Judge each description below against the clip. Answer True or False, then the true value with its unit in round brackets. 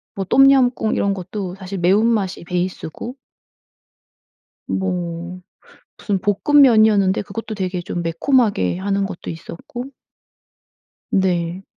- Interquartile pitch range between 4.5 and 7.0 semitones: False (3.4 semitones)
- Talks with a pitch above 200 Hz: False (195 Hz)